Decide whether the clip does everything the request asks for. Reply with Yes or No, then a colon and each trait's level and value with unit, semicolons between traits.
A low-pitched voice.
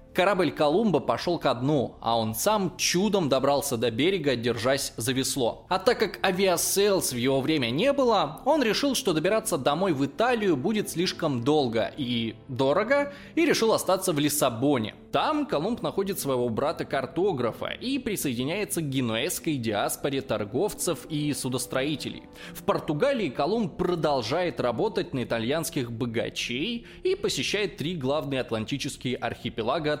No: medium, 150 Hz